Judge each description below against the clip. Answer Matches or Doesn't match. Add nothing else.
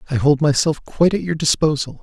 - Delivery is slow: Doesn't match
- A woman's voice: Doesn't match